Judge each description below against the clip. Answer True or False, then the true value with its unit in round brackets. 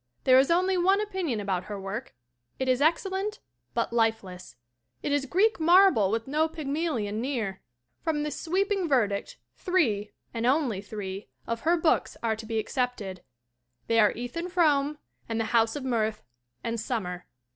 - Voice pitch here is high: True (250 Hz)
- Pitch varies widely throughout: True (7.1 semitones)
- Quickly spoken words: False (165 wpm)